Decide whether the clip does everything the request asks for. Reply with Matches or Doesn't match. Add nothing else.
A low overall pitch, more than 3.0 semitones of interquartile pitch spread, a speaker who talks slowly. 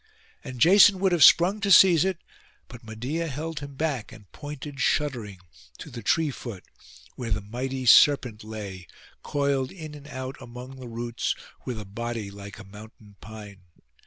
Doesn't match